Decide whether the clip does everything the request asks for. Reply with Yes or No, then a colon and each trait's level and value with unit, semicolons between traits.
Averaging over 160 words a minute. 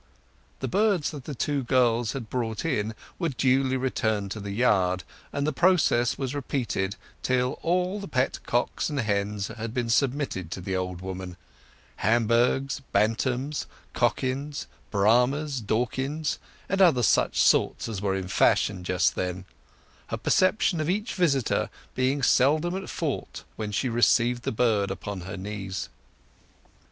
No: average, 145 wpm